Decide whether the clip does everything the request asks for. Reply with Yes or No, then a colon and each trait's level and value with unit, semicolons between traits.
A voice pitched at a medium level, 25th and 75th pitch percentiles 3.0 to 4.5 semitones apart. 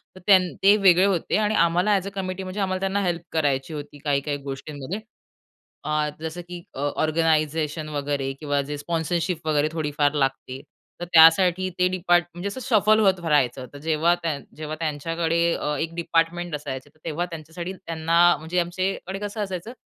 Yes: medium, 165 Hz; average, 3.5 semitones